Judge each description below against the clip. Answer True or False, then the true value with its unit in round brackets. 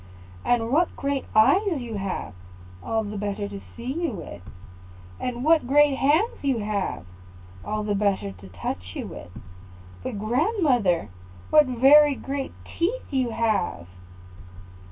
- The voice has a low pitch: False (235 Hz)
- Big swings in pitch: True (5.9 semitones)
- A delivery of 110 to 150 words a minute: True (135 wpm)